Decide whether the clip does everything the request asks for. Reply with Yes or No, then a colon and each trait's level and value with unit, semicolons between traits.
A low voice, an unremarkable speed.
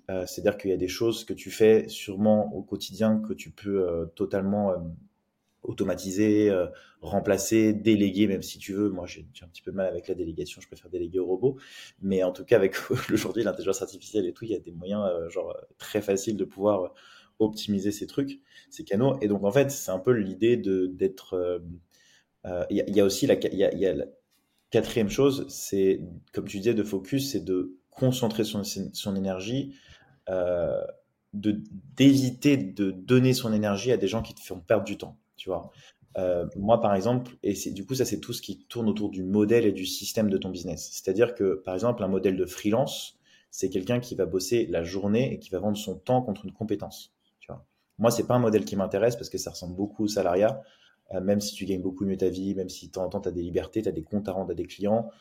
No: low, 100 Hz; fast, 235 wpm